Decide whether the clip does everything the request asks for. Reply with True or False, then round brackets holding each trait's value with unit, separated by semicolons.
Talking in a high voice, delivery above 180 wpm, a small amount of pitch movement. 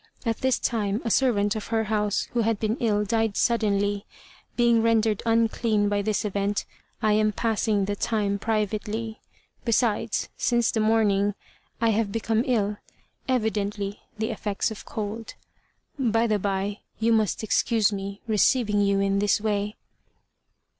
False (215 Hz; 145 wpm; 1.8 semitones)